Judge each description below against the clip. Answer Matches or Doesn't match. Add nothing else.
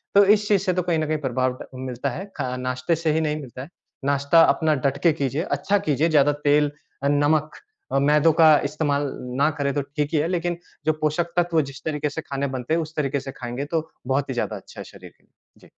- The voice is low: Doesn't match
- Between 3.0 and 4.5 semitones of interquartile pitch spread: Doesn't match